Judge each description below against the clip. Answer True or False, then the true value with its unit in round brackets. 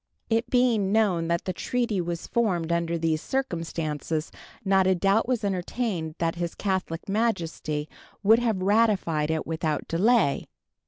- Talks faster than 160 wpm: False (145 wpm)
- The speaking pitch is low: False (185 Hz)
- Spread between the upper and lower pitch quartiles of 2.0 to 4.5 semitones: False (5.0 semitones)